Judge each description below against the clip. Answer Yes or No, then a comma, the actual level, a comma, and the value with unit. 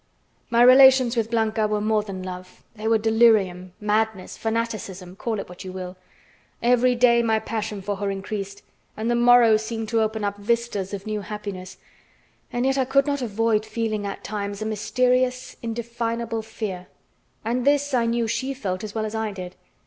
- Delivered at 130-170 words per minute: No, average, 180 wpm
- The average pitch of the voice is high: Yes, high, 220 Hz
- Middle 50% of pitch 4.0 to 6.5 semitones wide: No, narrow, 2.6 semitones